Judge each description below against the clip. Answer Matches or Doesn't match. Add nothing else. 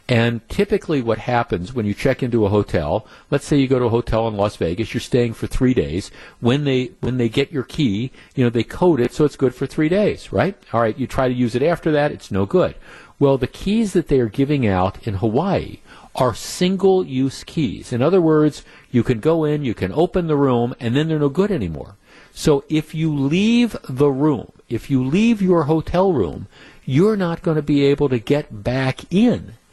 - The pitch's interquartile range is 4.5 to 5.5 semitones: Matches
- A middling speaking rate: Doesn't match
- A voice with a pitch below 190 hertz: Matches